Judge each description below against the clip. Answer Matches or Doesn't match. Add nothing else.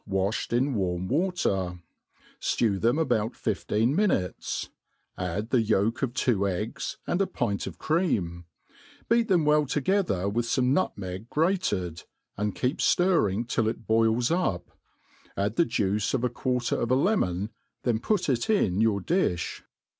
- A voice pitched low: Matches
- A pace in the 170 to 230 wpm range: Doesn't match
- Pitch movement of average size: Doesn't match